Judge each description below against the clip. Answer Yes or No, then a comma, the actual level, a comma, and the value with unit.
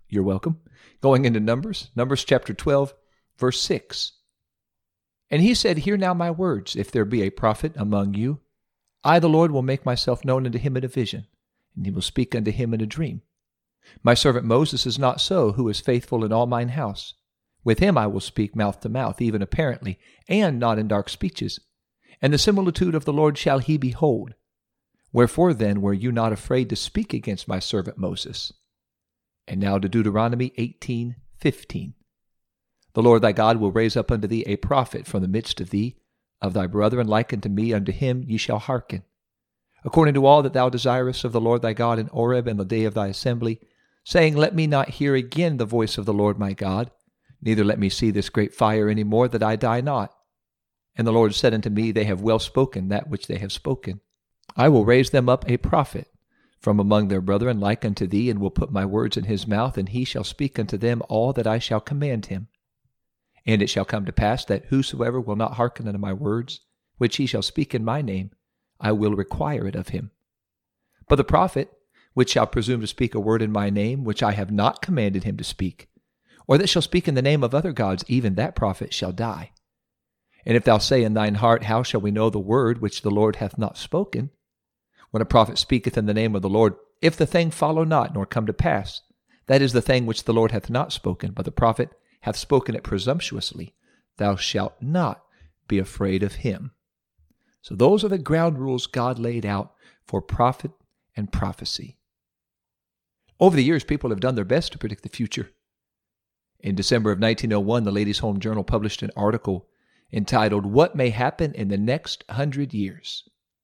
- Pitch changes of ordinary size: Yes, average, 4.0 semitones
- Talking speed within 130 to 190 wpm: No, fast, 205 wpm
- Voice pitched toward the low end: Yes, low, 115 Hz